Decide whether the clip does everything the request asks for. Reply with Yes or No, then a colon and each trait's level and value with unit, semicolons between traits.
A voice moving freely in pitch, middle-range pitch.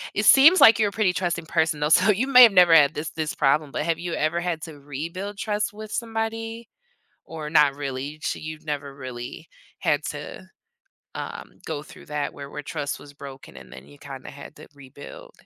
Yes: wide, 6.2 semitones; medium, 155 Hz